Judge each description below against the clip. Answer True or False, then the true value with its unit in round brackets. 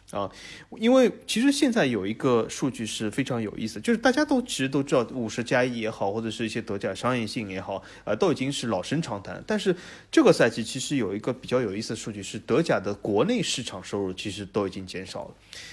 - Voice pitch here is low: True (120 Hz)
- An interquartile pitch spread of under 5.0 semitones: False (5.3 semitones)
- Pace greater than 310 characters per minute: True (350 characters per minute)